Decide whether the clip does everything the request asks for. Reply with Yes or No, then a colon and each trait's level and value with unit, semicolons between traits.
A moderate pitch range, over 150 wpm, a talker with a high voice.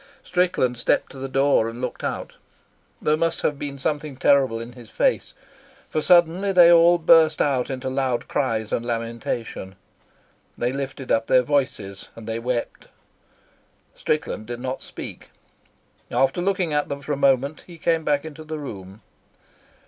No: average, 4.5 semitones; average, 160 wpm; low, 135 Hz